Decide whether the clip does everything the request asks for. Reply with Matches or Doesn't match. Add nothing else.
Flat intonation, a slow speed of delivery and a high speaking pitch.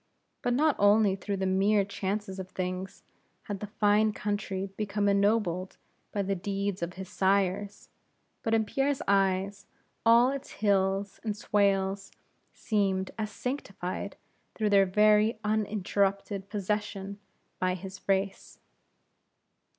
Matches